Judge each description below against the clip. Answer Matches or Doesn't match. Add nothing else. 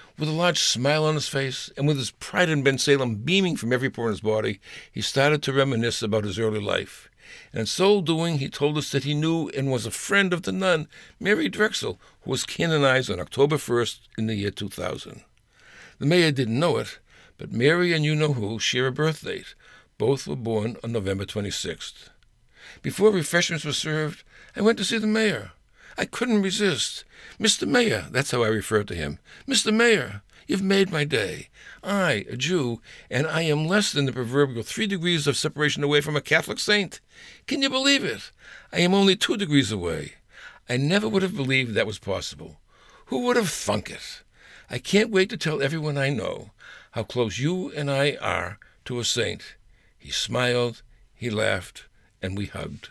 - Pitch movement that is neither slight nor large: Doesn't match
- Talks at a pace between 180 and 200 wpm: Matches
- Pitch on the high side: Doesn't match